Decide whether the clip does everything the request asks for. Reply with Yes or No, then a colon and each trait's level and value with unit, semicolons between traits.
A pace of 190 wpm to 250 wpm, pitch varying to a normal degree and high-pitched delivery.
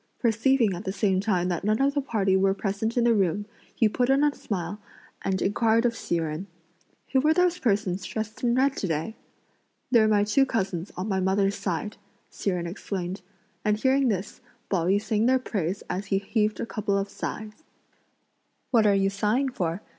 Yes: average, 195 wpm; average, 3.4 semitones; high, 210 Hz